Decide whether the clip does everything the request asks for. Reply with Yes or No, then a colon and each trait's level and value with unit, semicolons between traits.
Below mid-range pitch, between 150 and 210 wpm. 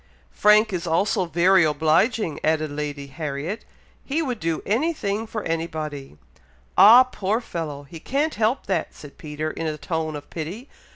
No: medium, 165 Hz; average, 160 wpm